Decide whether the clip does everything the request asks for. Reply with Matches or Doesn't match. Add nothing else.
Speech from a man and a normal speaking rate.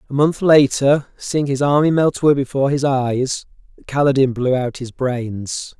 Matches